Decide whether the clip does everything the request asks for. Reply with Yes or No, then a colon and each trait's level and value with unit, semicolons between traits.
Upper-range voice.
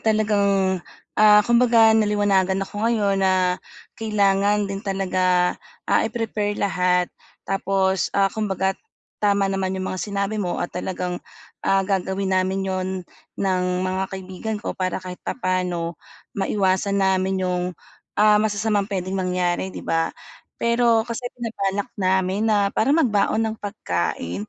Yes: high, 195 Hz